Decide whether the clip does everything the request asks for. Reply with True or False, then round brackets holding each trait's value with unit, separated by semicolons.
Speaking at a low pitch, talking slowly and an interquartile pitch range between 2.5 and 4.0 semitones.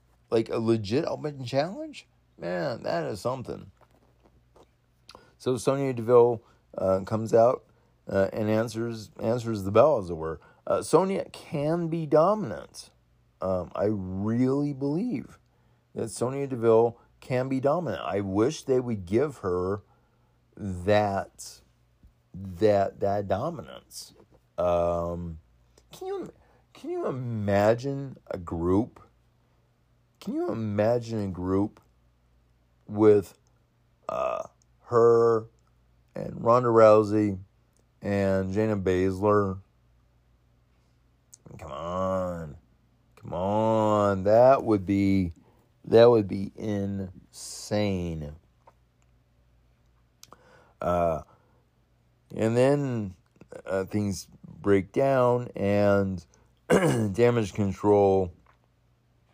False (105 Hz; 95 wpm; 4.7 semitones)